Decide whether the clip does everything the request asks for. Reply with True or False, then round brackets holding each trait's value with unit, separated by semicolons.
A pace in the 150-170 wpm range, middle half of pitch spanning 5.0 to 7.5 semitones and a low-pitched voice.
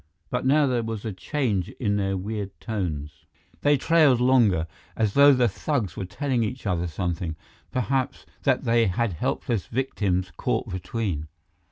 True (155 wpm; 5.4 semitones; 110 Hz)